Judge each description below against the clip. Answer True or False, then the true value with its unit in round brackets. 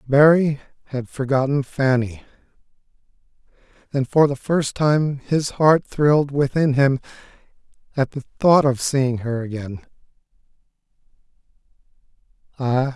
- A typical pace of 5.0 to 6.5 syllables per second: False (4.3 syllables/s)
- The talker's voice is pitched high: False (135 Hz)